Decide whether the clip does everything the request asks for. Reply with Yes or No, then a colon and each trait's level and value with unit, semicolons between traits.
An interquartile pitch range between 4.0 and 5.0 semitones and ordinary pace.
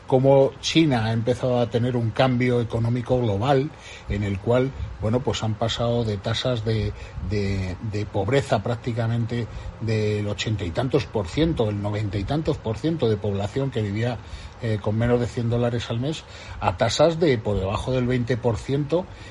No: average, 3.3 semitones; average, 175 wpm